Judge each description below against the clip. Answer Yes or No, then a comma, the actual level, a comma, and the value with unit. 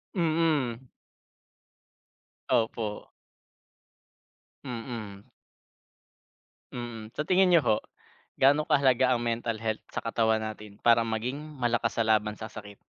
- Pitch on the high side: No, low, 115 Hz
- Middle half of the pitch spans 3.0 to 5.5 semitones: Yes, average, 3.3 semitones